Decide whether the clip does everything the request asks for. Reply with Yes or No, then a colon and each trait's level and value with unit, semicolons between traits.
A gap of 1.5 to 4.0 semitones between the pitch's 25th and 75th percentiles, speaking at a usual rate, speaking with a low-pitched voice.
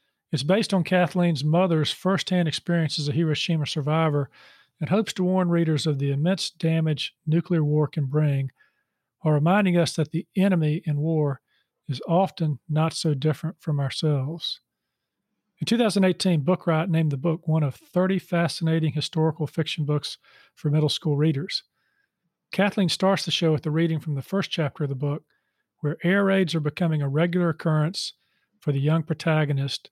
No: average, 2.8 semitones; average, 165 wpm; medium, 160 Hz